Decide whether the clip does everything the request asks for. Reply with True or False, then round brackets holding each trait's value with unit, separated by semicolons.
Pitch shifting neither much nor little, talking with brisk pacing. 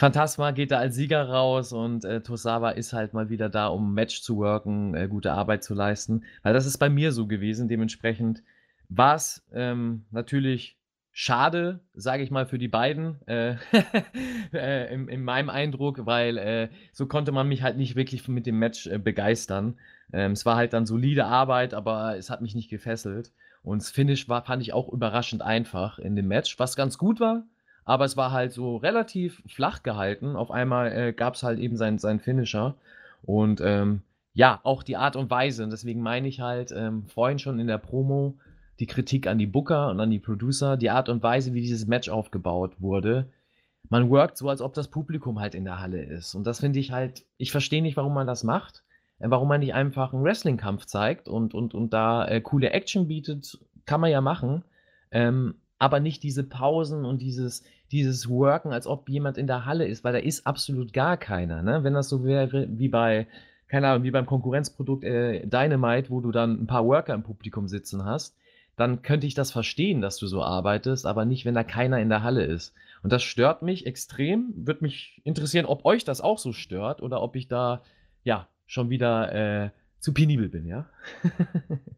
True (3.7 semitones; 205 wpm)